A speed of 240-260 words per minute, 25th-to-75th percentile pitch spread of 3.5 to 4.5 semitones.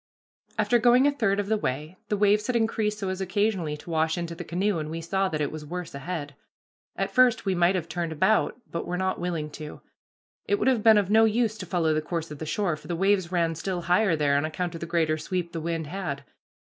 Yes: fast, 250 wpm; average, 4.2 semitones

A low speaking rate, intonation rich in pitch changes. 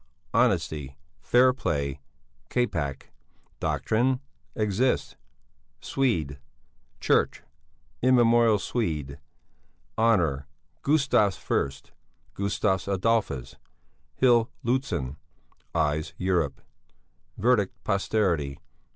Yes: slow, 65 wpm; wide, 8.4 semitones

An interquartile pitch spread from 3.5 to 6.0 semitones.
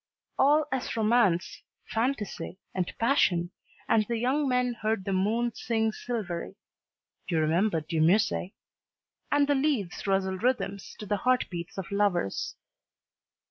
Yes: average, 4.7 semitones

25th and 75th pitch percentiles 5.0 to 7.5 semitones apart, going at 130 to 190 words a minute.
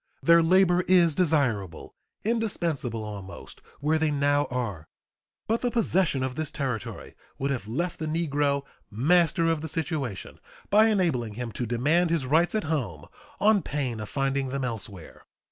Yes: wide, 5.5 semitones; average, 155 wpm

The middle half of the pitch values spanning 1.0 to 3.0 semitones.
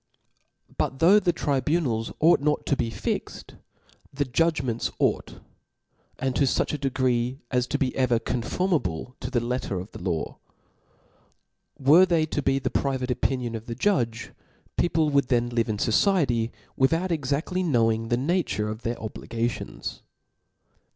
No: average, 4.4 semitones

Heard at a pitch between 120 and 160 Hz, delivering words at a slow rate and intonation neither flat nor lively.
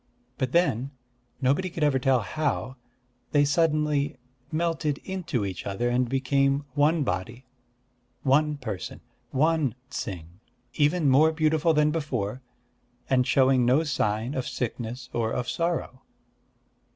Yes: low, 135 Hz; slow, 125 wpm; average, 3.7 semitones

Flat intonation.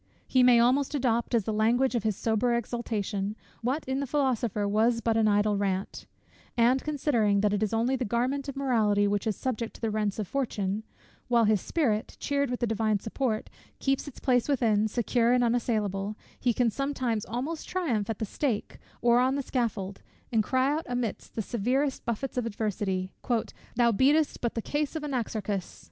No: average, 3.5 semitones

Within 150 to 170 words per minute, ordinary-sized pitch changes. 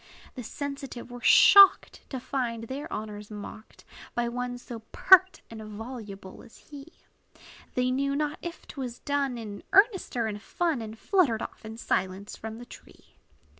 Yes: average, 165 wpm; average, 4.2 semitones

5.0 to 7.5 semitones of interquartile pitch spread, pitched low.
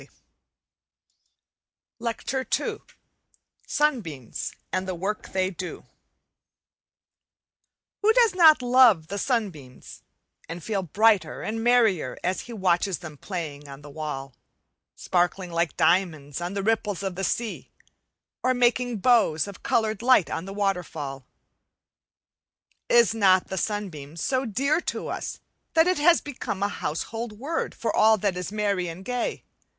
No: wide, 5.5 semitones; high, 200 Hz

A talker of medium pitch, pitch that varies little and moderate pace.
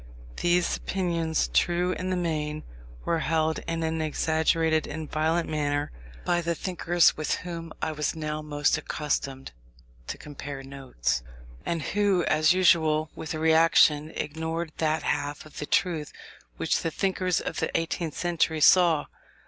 Yes: medium, 160 Hz; narrow, 2.0 semitones; average, 150 wpm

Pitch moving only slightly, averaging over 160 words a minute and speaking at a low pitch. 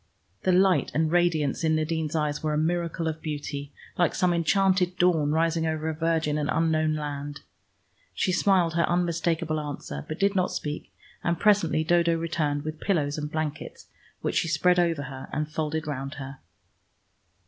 No: narrow, 2.3 semitones; average, 170 wpm; medium, 160 Hz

